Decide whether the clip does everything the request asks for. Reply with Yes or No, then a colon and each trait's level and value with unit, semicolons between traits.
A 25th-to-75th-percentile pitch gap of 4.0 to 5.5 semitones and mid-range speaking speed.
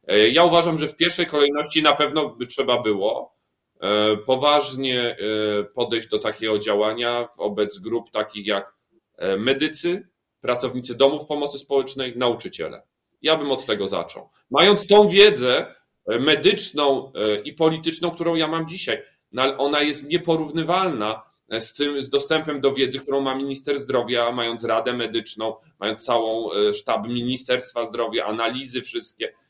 Yes: average, 5.1 semitones; average, 130 wpm